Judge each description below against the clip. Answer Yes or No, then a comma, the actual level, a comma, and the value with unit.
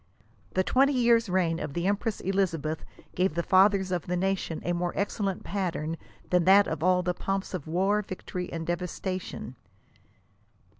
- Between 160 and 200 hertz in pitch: Yes, medium, 185 Hz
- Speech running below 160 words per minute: No, average, 180 wpm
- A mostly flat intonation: Yes, narrow, 2.2 semitones